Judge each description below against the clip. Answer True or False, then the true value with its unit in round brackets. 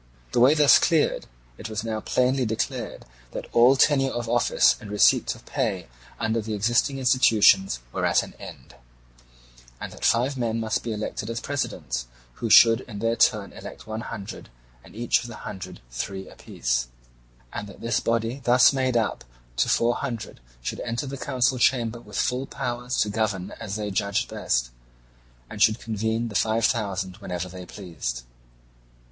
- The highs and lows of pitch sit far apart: False (3.2 semitones)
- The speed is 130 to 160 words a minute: False (170 wpm)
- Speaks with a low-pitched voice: True (115 Hz)